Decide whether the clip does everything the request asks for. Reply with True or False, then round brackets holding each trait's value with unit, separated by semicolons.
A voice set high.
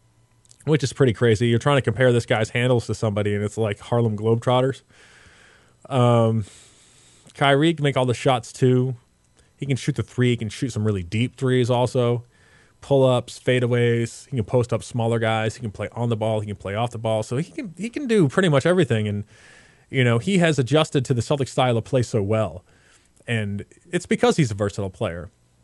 False (120 Hz)